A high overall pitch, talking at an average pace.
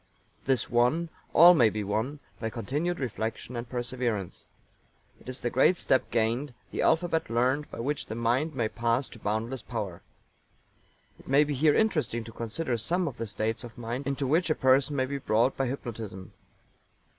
No: low, 125 Hz; average, 180 wpm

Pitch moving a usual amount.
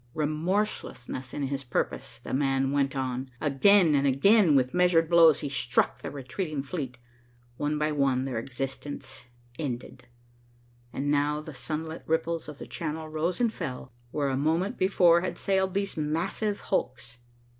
Yes: average, 3.8 semitones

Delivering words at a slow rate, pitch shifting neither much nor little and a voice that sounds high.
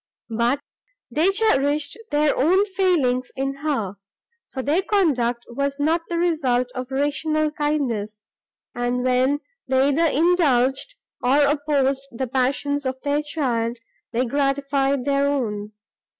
Yes: slow, 125 wpm; average, 3.0 semitones; very high, 275 Hz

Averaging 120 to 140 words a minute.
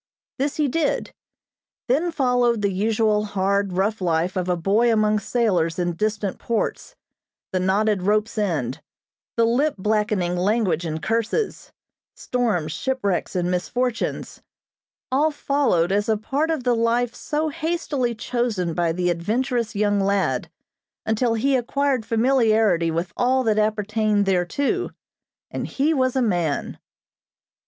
Yes: slow, 135 wpm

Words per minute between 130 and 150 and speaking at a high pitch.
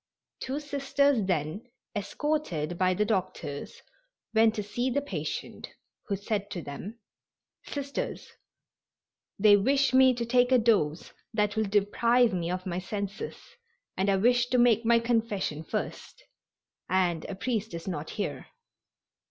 Yes: average, 140 wpm; high, 210 Hz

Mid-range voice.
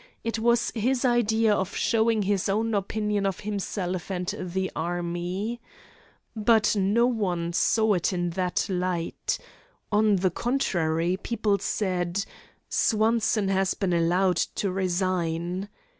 No: high, 195 Hz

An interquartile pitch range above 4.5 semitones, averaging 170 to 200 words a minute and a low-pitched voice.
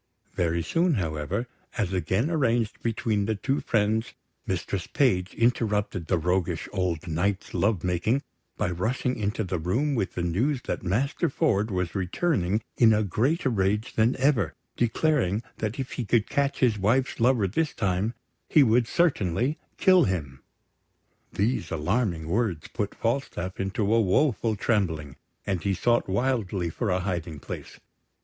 No: average, 5.0 semitones; average, 150 wpm; low, 105 Hz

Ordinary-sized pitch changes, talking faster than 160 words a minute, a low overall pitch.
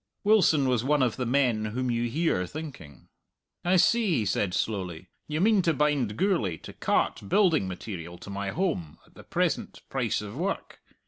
No: wide, 8.4 semitones; average, 180 wpm; low, 125 Hz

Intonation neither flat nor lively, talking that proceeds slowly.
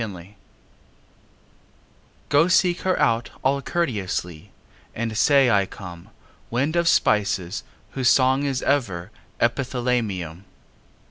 No: wide, 6.0 semitones; slow, 105 wpm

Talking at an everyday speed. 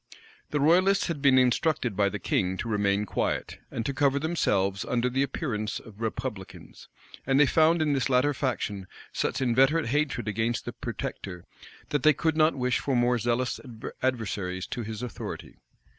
Yes: average, 170 wpm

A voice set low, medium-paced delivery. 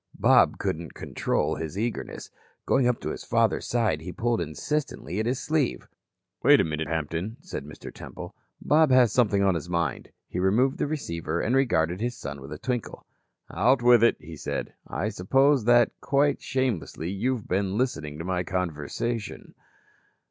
Yes: low, 105 Hz; average, 170 wpm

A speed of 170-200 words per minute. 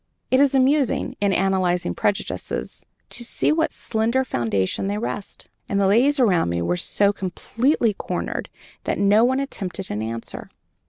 No: average, 160 wpm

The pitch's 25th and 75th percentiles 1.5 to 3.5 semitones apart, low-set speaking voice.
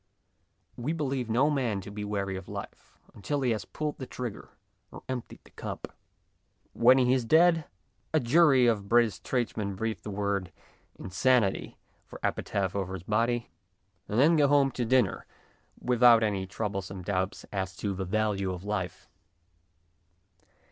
No: average, 4.6 semitones; low, 110 Hz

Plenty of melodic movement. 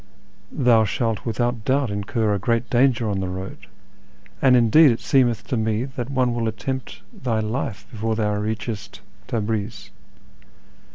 No: average, 2.9 semitones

